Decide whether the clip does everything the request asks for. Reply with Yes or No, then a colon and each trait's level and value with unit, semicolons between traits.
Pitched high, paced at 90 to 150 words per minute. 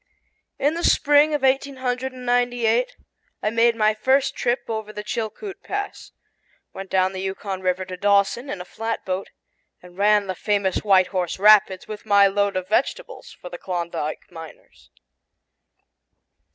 Yes: high, 210 Hz; average, 145 wpm